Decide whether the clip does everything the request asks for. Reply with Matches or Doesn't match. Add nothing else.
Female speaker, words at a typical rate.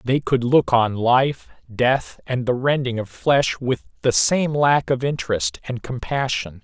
Doesn't match